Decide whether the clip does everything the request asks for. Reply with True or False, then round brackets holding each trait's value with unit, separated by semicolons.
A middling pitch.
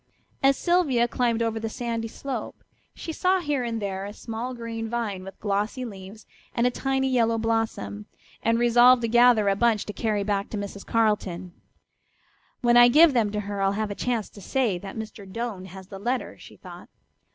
False (225 Hz)